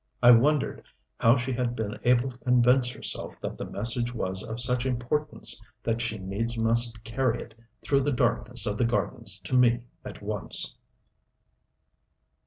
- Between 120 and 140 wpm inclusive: No, average, 160 wpm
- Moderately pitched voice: No, low, 120 Hz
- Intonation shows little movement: Yes, narrow, 1.7 semitones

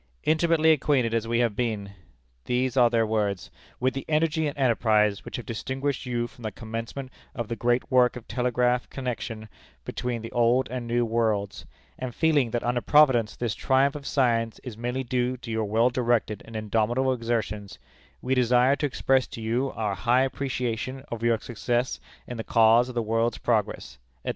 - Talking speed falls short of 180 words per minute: No, average, 185 wpm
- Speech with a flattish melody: Yes, narrow, 2.3 semitones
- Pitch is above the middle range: No, low, 120 Hz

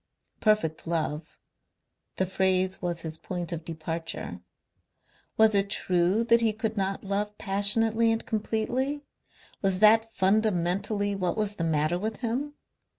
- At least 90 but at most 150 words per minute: Yes, slow, 135 wpm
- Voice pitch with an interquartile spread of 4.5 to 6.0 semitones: No, average, 4.1 semitones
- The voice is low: No, high, 200 Hz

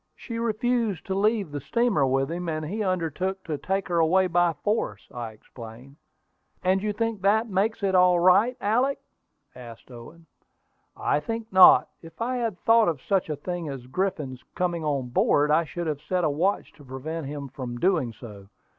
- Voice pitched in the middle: Yes, medium, 175 Hz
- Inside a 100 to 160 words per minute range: No, average, 185 wpm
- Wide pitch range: Yes, wide, 5.9 semitones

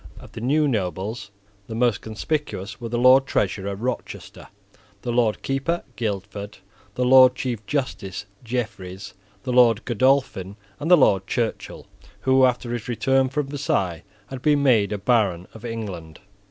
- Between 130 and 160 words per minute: Yes, average, 150 wpm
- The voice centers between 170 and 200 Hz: No, low, 120 Hz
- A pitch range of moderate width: Yes, average, 4.5 semitones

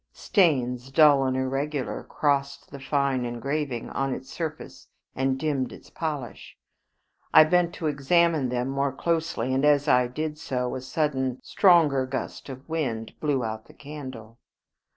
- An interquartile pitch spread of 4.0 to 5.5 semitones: No, average, 2.8 semitones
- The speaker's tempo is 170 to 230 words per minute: No, average, 150 wpm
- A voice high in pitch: No, medium, 140 Hz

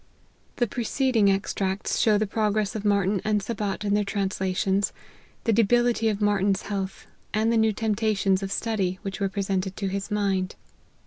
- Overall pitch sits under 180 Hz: No, high, 205 Hz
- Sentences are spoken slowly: No, average, 165 wpm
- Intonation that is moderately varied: No, narrow, 1.9 semitones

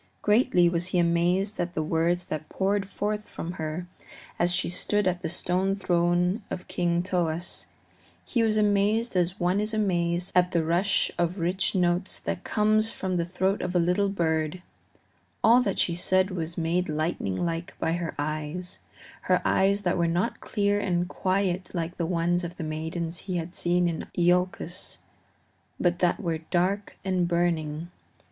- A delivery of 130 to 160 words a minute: No, average, 170 wpm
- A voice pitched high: No, medium, 175 Hz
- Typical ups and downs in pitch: No, narrow, 2.1 semitones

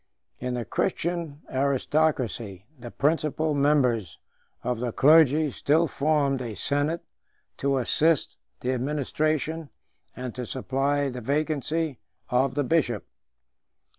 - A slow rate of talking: Yes, slow, 110 wpm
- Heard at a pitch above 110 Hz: Yes, medium, 140 Hz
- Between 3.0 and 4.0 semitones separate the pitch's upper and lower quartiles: Yes, average, 3.6 semitones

